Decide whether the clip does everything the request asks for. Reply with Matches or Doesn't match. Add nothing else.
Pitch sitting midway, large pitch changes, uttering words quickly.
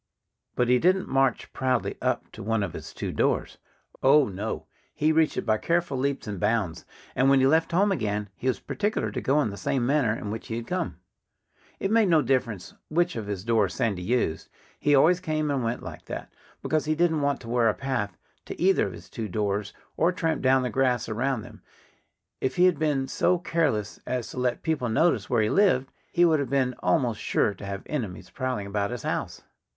Doesn't match